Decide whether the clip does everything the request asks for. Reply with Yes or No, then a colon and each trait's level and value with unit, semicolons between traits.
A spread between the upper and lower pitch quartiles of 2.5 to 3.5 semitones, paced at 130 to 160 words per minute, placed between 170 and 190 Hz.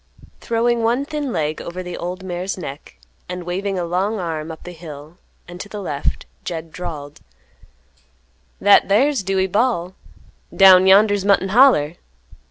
Yes: average, 3.2 semitones; average, 150 wpm; medium, 185 Hz